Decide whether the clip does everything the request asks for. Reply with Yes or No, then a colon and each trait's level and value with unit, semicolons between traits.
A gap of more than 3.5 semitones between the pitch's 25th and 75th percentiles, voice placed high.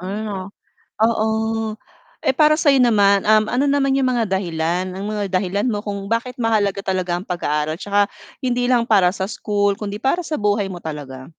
Yes: average, 3.9 semitones; high, 205 Hz